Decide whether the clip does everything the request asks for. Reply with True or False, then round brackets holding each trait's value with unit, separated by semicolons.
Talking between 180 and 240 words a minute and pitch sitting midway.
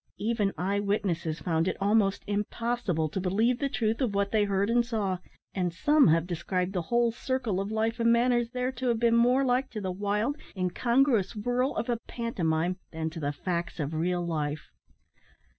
False (190 wpm; 205 Hz)